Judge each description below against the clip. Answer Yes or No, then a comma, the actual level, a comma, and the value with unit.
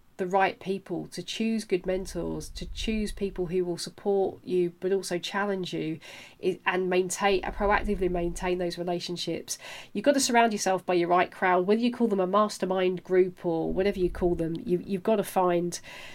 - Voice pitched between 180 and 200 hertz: Yes, medium, 185 Hz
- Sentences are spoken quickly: No, average, 185 wpm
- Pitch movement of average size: No, narrow, 2.0 semitones